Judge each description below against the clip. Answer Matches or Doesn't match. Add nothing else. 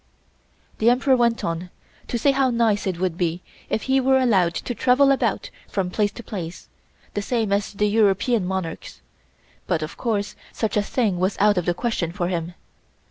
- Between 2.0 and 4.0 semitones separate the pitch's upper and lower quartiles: Doesn't match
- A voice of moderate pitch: Doesn't match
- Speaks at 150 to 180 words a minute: Doesn't match